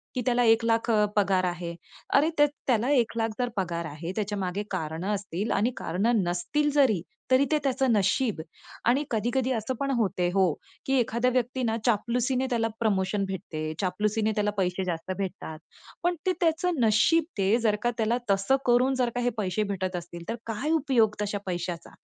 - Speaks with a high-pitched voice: Yes, high, 220 Hz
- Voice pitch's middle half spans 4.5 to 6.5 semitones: Yes, average, 4.8 semitones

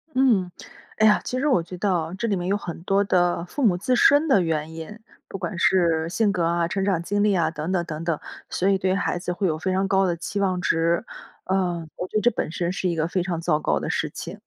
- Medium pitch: Yes, medium, 180 Hz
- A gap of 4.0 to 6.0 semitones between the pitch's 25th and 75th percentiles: No, average, 2.8 semitones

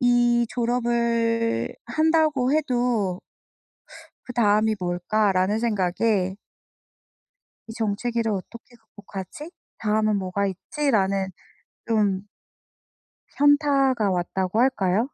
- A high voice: Yes, high, 225 Hz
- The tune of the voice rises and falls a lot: No, average, 3.9 semitones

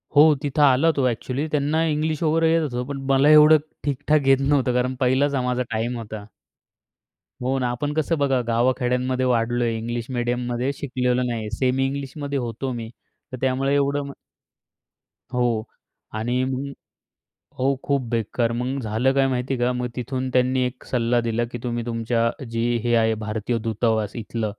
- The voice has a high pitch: No, low, 125 Hz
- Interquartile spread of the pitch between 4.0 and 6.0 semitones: No, narrow, 2.6 semitones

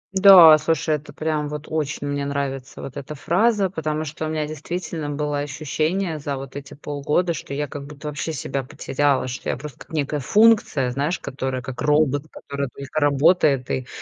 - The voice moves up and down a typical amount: No, narrow, 2.1 semitones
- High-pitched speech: No, medium, 145 Hz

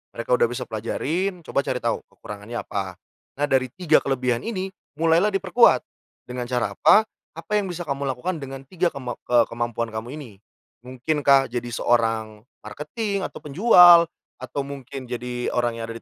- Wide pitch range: Yes, wide, 6.3 semitones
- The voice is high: No, low, 135 Hz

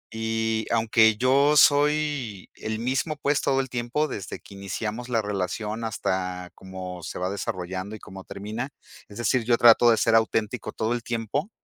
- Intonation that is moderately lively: Yes, average, 3.5 semitones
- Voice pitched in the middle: No, low, 110 Hz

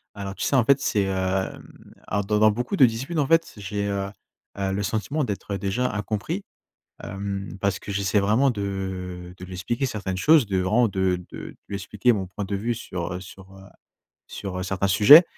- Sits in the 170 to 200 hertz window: No, low, 100 Hz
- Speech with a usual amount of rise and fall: Yes, average, 3.1 semitones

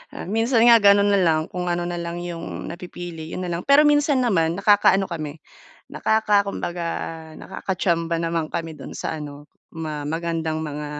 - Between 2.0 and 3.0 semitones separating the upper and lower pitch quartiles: No, average, 3.7 semitones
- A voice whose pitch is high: No, medium, 175 Hz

